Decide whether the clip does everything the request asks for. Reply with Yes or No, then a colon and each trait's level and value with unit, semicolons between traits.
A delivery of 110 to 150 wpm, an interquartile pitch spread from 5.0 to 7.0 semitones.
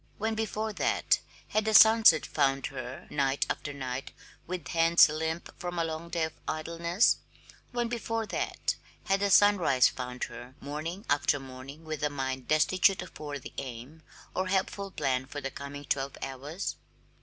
No: average, 160 wpm; wide, 5.5 semitones